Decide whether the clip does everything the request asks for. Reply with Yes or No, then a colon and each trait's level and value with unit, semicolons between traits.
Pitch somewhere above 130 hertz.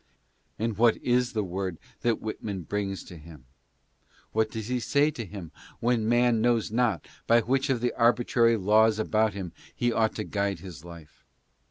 No: low, 110 Hz